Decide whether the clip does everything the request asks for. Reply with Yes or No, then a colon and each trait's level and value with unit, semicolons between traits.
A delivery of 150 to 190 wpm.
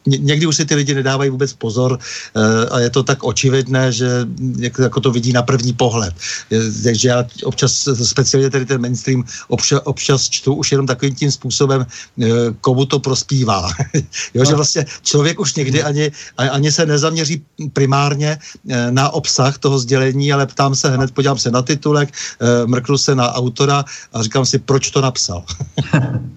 Yes: fast, 170 wpm